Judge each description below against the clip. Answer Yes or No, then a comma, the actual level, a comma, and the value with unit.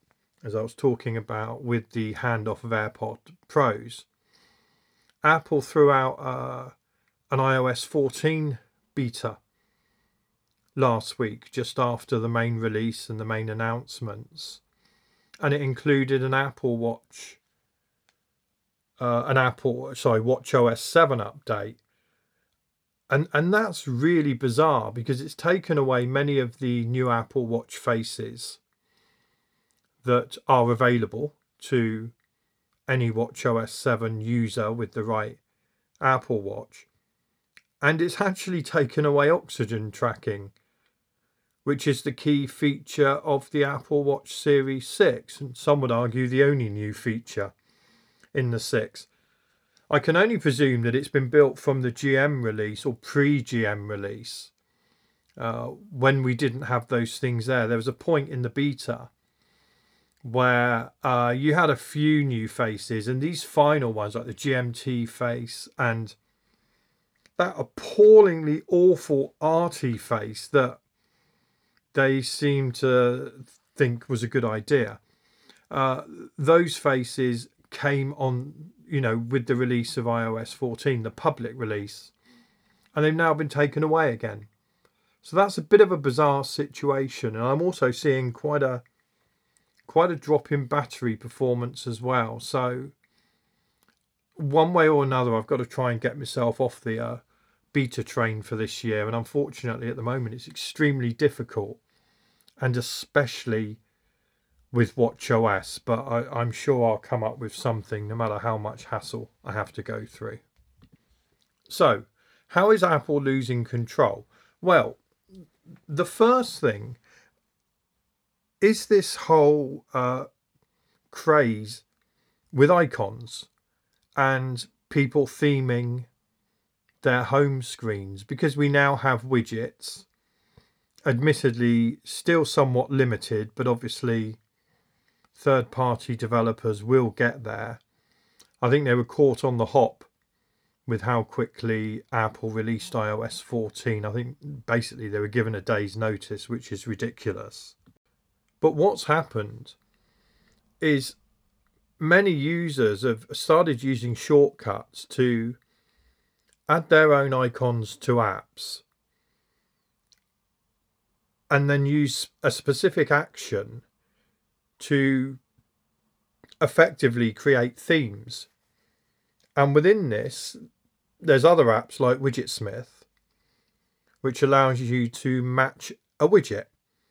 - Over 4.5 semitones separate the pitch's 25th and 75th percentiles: No, average, 3.7 semitones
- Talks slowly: Yes, slow, 125 wpm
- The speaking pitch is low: Yes, low, 125 Hz